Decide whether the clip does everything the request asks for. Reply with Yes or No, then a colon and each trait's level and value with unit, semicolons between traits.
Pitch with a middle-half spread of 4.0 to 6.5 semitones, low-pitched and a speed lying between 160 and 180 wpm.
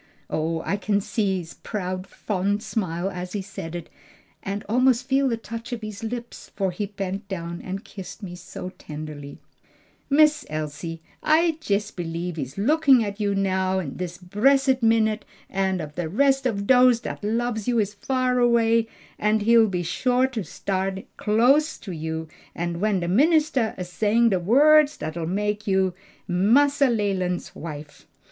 No: average, 4.8 semitones; high, 205 Hz; average, 165 wpm